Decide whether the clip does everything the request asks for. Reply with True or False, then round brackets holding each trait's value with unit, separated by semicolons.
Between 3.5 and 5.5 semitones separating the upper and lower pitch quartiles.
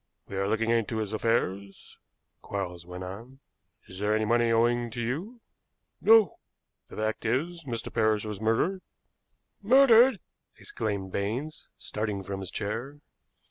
True (4.7 semitones)